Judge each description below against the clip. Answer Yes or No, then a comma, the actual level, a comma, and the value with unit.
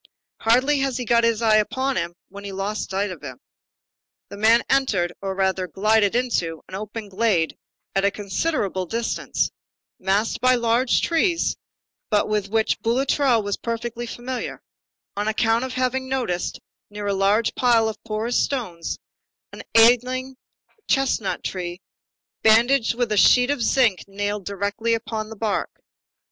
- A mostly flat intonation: No, average, 3.5 semitones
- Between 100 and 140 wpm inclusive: No, average, 150 wpm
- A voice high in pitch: Yes, high, 220 Hz